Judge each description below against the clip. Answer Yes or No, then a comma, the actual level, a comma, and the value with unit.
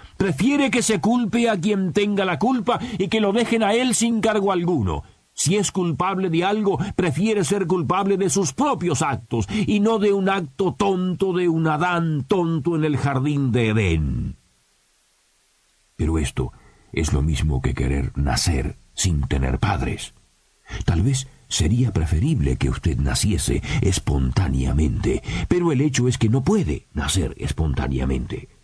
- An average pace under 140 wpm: No, average, 155 wpm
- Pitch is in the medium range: Yes, medium, 170 Hz